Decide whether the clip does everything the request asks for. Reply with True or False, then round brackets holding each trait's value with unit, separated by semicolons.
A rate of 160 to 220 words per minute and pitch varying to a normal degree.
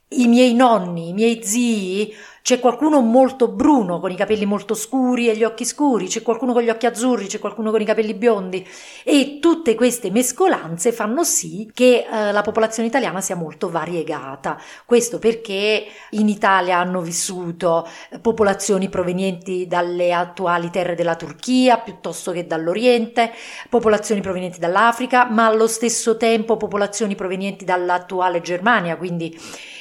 False (145 wpm; 4.5 semitones)